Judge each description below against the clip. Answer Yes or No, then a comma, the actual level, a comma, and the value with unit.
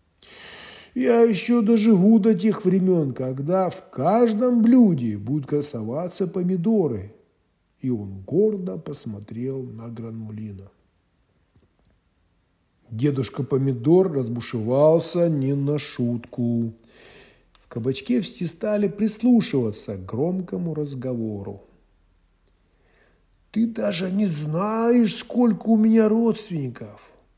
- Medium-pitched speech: Yes, medium, 145 Hz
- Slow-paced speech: Yes, slow, 90 wpm